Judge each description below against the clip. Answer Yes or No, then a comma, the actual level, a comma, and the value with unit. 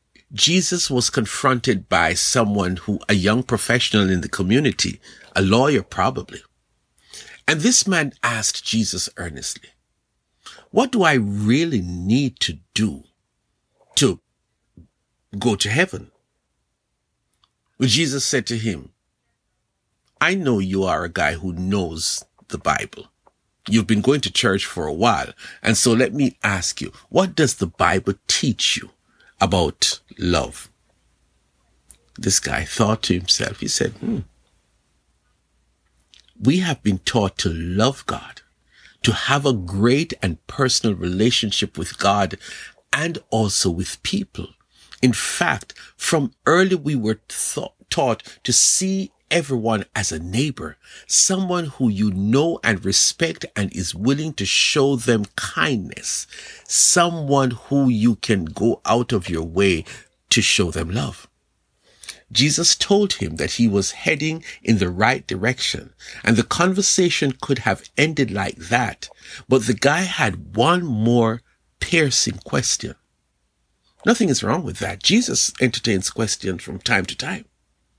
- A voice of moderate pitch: No, low, 115 Hz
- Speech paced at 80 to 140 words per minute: Yes, slow, 135 wpm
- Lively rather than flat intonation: Yes, wide, 6.2 semitones